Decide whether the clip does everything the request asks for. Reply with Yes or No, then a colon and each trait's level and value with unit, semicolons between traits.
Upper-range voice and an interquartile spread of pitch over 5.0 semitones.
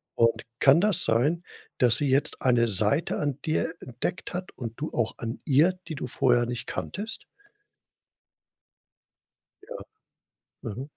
No: low, 130 Hz; wide, 5.4 semitones